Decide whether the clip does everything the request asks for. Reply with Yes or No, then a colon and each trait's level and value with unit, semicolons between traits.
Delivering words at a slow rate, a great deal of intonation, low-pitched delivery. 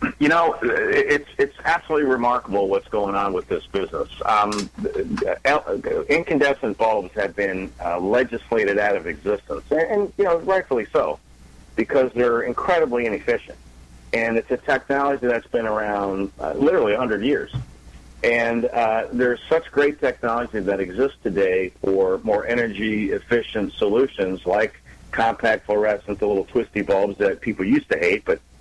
No: average, 150 wpm; wide, 8.8 semitones; low, 120 Hz